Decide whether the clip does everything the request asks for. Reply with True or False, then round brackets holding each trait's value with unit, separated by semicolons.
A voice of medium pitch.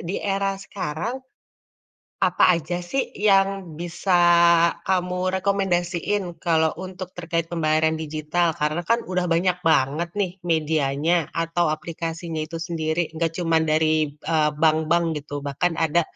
True (165 Hz)